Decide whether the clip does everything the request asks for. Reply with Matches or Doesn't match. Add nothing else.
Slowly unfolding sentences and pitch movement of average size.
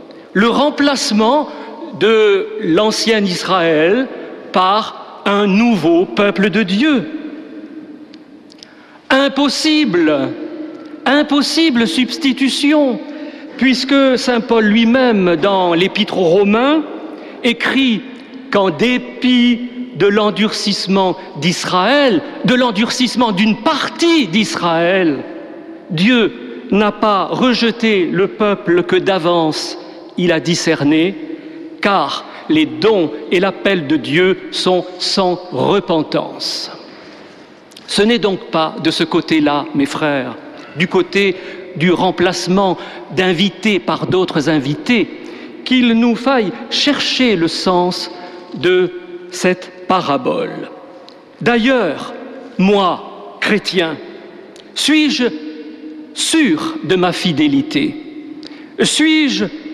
Doesn't match